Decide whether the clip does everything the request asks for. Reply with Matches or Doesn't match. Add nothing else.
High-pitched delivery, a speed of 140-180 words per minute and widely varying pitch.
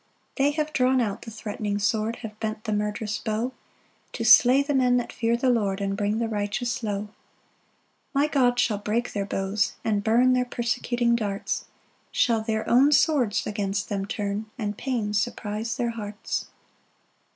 Doesn't match